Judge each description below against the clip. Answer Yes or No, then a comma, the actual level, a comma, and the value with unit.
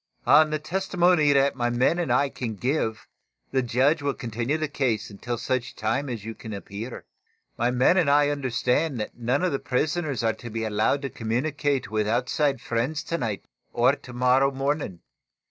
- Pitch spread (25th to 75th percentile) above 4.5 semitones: No, average, 3.9 semitones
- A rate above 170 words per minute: Yes, average, 180 wpm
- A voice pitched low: Yes, low, 130 Hz